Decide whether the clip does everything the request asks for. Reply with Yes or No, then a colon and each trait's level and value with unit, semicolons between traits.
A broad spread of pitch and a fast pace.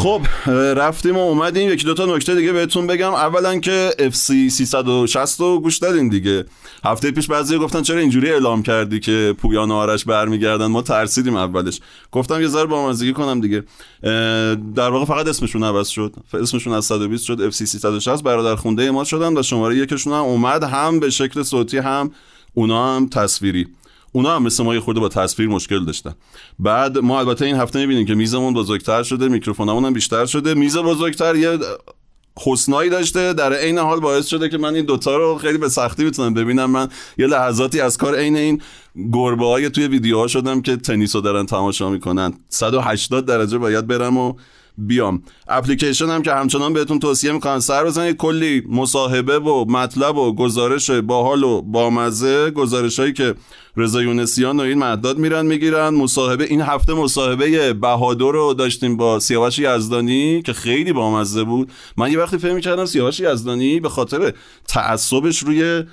No: average, 4.7 semitones; fast, 175 wpm